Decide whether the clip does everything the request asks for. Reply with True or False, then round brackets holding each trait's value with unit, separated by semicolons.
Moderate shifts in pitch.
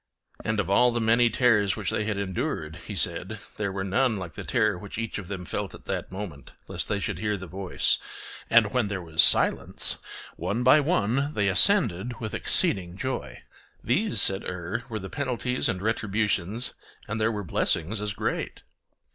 True (3.7 semitones)